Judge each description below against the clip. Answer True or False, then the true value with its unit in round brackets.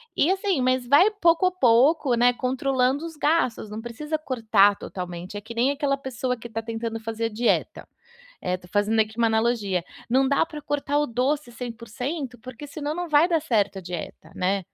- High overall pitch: True (245 Hz)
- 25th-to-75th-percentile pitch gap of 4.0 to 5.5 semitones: True (4.7 semitones)